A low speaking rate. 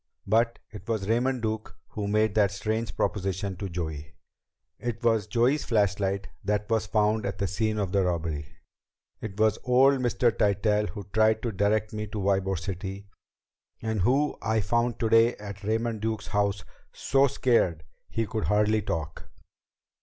No: average, 160 wpm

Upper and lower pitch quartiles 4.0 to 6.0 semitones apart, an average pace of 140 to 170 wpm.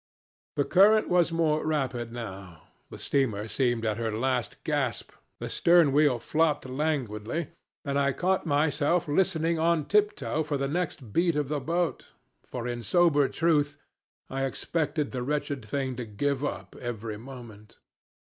Yes: average, 4.8 semitones; average, 150 wpm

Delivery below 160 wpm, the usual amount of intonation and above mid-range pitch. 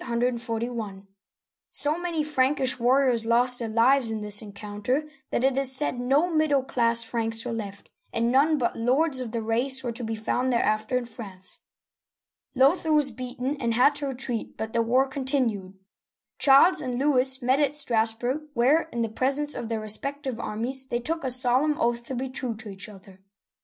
No: average, 180 wpm; average, 3.2 semitones; very high, 250 Hz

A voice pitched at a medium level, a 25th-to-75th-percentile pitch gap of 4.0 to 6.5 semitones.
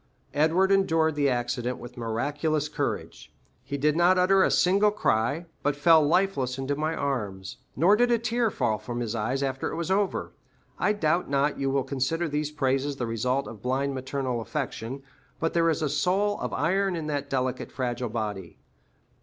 Yes: medium, 145 Hz; average, 4.8 semitones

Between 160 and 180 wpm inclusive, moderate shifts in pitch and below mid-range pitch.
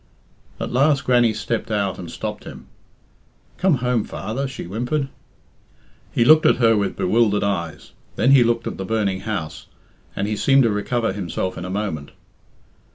Yes: average, 165 wpm; average, 4.0 semitones; low, 110 Hz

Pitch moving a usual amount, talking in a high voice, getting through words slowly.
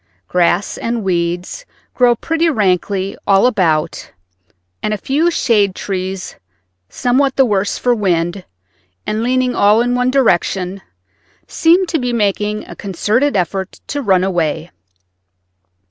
Yes: average, 4.9 semitones; high, 210 Hz; slow, 130 wpm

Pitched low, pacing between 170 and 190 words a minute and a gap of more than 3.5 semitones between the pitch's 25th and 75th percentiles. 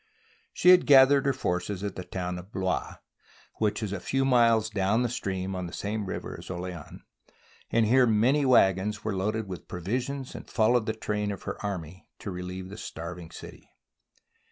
Yes: low, 105 Hz; average, 180 wpm; average, 4.1 semitones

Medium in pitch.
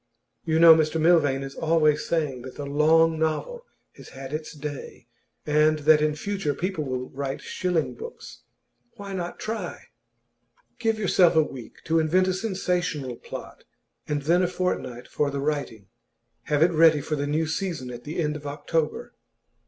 Yes: medium, 155 Hz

